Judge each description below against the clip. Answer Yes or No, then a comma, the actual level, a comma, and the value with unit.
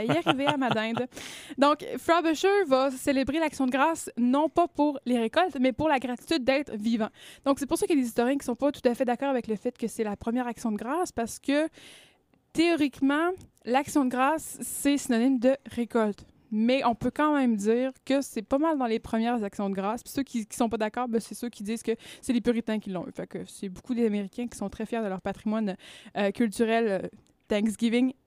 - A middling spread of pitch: Yes, average, 3.7 semitones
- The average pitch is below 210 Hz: No, high, 245 Hz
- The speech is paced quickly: Yes, fast, 235 wpm